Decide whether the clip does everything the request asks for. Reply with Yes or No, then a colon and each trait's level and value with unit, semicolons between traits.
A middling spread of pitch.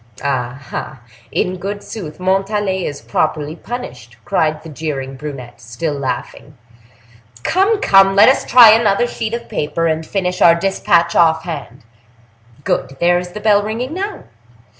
No: wide, 6.3 semitones